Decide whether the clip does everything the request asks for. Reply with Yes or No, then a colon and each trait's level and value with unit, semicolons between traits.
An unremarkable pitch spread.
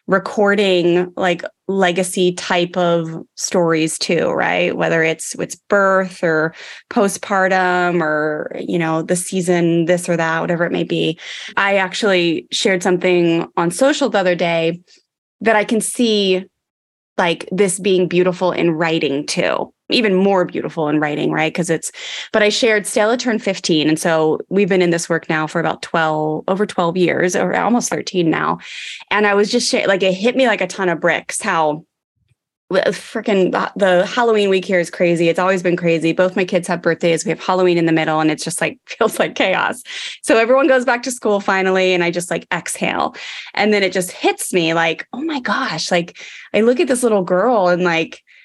Yes: average, 3.2 semitones